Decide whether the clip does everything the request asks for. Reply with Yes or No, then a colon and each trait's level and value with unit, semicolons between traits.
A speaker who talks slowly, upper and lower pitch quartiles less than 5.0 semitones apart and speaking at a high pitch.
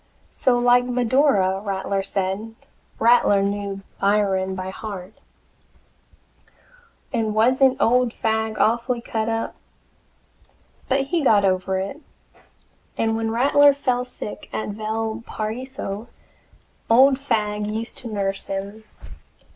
Yes: slow, 105 wpm; average, 3.5 semitones; high, 220 Hz